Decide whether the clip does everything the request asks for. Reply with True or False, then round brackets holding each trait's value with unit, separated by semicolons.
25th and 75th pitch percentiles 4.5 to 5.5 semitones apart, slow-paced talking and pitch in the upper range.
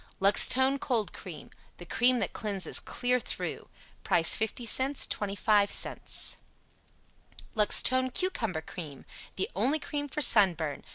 True (5.2 semitones; 110 wpm; 220 Hz)